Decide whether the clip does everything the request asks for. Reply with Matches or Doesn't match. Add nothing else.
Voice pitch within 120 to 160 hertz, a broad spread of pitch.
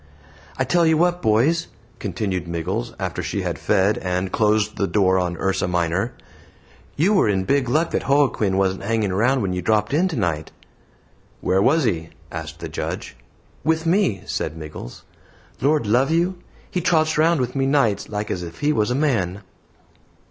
Doesn't match